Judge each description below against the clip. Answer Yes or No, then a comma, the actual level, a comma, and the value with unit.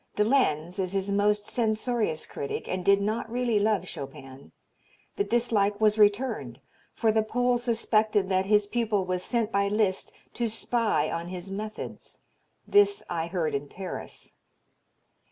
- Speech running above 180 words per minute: No, average, 150 wpm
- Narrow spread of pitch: No, average, 3.4 semitones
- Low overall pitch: No, high, 210 Hz